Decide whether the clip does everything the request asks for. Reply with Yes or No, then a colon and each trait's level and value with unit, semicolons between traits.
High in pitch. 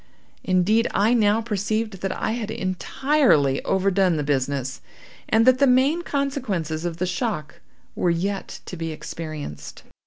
Yes: high, 195 Hz